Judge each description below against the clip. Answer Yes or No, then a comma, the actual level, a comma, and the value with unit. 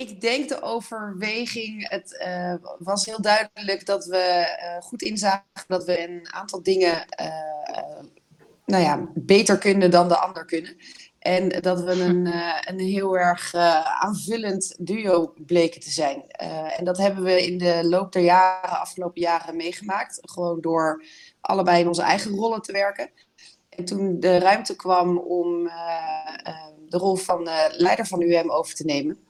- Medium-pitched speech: Yes, medium, 180 Hz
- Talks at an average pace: Yes, average, 170 wpm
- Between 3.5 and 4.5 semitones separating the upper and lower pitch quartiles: No, narrow, 2.4 semitones